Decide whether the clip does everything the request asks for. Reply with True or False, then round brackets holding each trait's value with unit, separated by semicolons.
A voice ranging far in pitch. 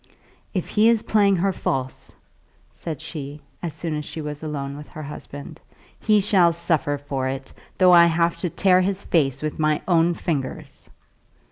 False (3.8 semitones)